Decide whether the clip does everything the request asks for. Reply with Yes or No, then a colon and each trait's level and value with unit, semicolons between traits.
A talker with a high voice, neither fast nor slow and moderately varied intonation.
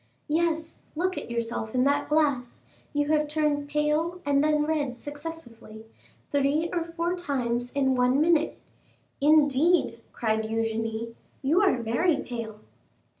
No: very high, 290 Hz; slow, 130 wpm; average, 4.7 semitones